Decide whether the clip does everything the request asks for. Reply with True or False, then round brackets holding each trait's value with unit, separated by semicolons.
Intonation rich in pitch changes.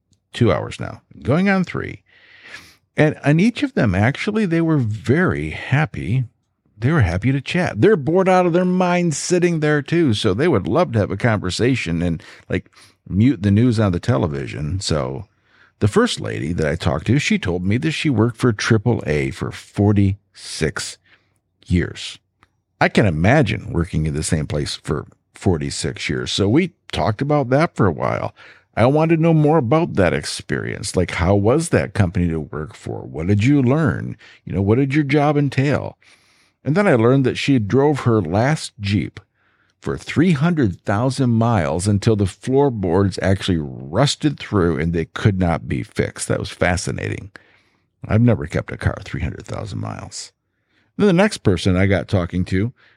True (7.7 semitones)